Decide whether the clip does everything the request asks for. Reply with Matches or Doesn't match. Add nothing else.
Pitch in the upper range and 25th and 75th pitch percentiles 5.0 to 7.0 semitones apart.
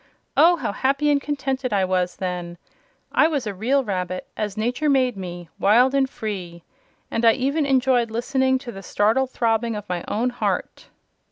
Matches